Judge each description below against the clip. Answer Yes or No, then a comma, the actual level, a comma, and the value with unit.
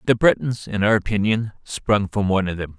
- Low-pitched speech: Yes, low, 105 Hz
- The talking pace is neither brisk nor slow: No, fast, 215 wpm